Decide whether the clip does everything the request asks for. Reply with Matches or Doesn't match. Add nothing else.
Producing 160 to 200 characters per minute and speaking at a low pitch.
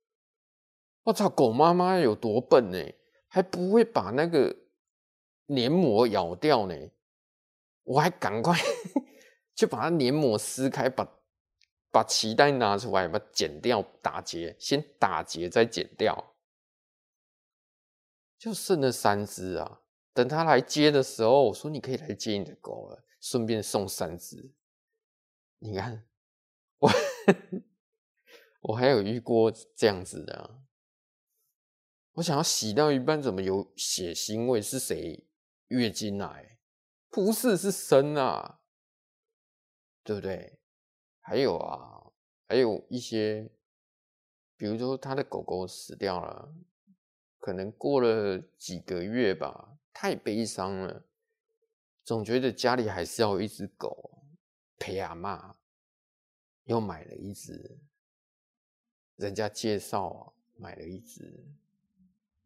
Matches